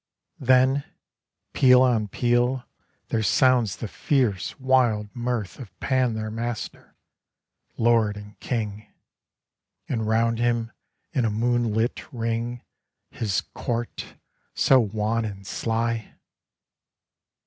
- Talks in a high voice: No, low, 115 Hz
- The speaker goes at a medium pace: No, slow, 105 wpm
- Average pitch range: No, narrow, 2.2 semitones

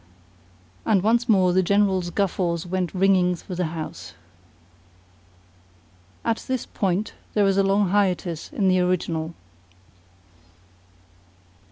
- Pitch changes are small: Yes, narrow, 2.2 semitones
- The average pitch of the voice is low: No, medium, 185 Hz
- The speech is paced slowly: Yes, slow, 115 wpm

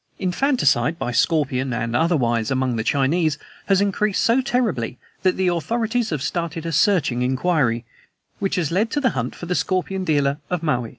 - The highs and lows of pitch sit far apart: Yes, wide, 6.5 semitones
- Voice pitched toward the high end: No, medium, 165 Hz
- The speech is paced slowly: No, average, 175 wpm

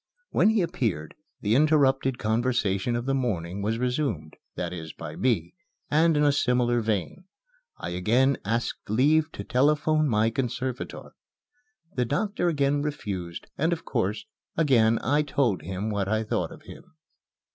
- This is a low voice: Yes, low, 125 Hz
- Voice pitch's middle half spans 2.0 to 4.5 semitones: No, wide, 5.4 semitones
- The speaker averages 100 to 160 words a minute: Yes, average, 150 wpm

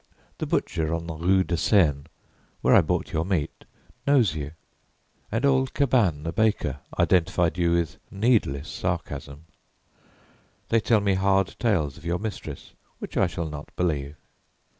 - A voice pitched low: Yes, very low, 85 Hz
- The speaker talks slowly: No, average, 150 wpm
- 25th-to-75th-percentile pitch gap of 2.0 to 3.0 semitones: No, average, 4.9 semitones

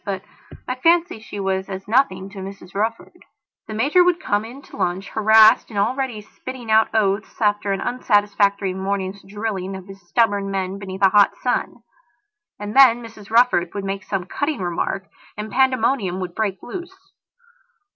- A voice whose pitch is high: Yes, high, 205 Hz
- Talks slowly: No, average, 165 wpm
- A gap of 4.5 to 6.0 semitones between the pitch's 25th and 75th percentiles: No, average, 3.4 semitones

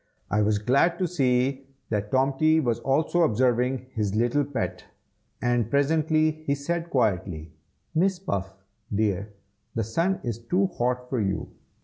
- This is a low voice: Yes, low, 130 Hz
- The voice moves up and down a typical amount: No, wide, 6.1 semitones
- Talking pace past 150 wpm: No, average, 140 wpm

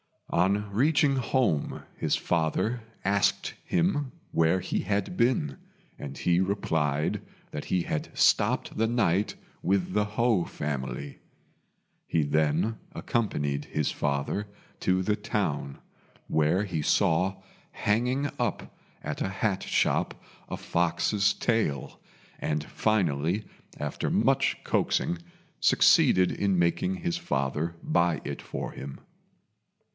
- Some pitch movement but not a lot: No, wide, 5.9 semitones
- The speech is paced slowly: Yes, slow, 115 wpm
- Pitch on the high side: No, very low, 95 Hz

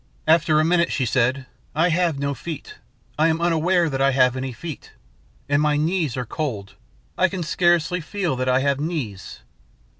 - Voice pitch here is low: No, medium, 150 Hz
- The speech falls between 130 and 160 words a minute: No, average, 180 wpm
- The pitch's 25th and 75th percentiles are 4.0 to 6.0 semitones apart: Yes, average, 4.4 semitones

